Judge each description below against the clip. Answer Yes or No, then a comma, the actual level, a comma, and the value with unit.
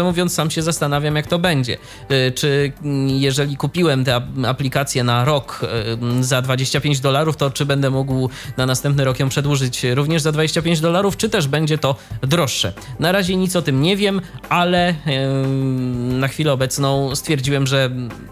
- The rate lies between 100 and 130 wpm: No, average, 155 wpm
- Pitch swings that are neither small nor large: Yes, average, 3.1 semitones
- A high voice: No, medium, 140 Hz